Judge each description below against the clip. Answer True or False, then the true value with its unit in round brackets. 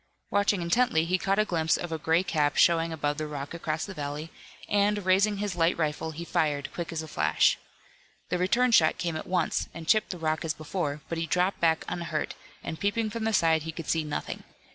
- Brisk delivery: True (220 wpm)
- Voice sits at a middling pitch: True (165 Hz)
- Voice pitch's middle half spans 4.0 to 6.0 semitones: False (3.2 semitones)